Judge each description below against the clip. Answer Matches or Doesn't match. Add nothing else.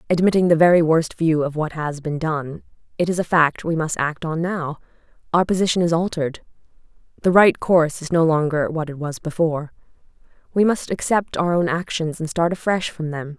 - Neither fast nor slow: Matches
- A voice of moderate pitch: Matches